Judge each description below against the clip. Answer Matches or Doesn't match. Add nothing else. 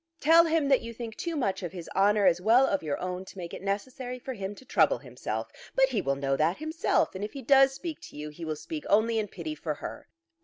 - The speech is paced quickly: Matches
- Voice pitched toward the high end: Matches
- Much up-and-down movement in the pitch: Matches